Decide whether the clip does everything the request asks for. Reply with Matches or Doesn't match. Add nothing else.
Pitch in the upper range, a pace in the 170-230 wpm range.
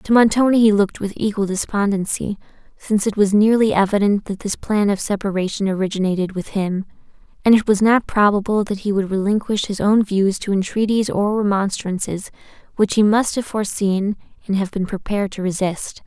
Matches